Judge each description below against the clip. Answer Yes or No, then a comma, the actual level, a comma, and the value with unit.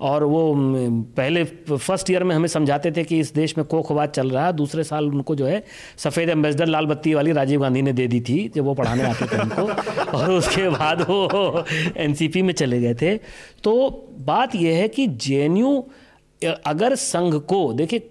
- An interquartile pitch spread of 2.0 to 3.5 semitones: No, average, 4.0 semitones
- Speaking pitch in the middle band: Yes, medium, 160 Hz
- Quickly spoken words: No, average, 190 wpm